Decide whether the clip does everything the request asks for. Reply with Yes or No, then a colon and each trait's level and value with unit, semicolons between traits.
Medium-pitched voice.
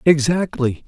Yes: medium, 145 Hz